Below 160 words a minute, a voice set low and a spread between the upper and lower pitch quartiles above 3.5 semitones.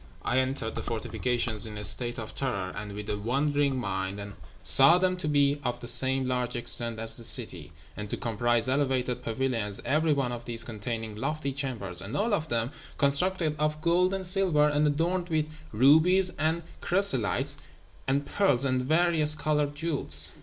No: average, 175 wpm; low, 130 Hz; average, 4.9 semitones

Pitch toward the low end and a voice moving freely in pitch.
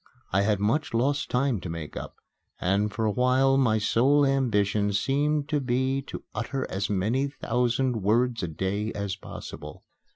No: low, 115 Hz; average, 4.8 semitones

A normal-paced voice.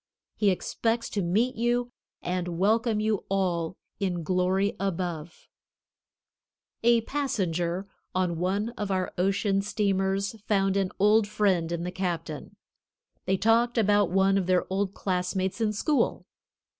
No: slow, 130 wpm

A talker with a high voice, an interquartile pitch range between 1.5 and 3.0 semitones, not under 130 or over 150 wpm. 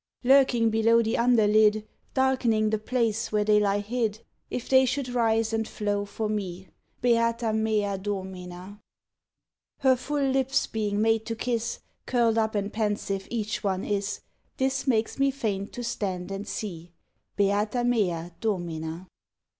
Yes: high, 220 Hz; narrow, 2.6 semitones; average, 145 wpm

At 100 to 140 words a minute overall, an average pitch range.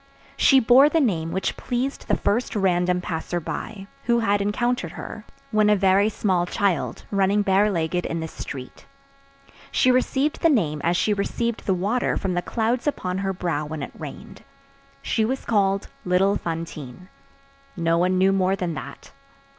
No: average, 170 wpm; average, 4.0 semitones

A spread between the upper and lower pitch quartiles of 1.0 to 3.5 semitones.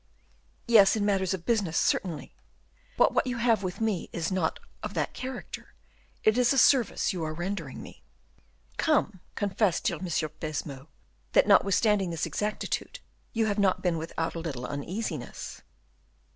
No: average, 5.0 semitones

